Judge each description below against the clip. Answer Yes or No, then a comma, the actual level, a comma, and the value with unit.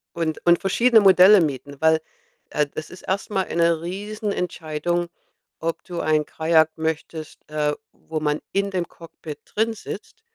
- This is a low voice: No, medium, 170 Hz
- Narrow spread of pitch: No, average, 3.5 semitones